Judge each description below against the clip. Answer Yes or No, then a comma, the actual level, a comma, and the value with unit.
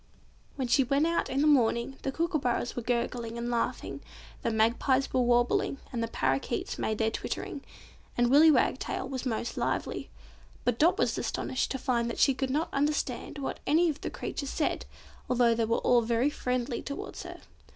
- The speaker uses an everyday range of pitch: Yes, average, 3.0 semitones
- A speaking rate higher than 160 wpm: Yes, average, 180 wpm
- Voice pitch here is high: Yes, very high, 250 Hz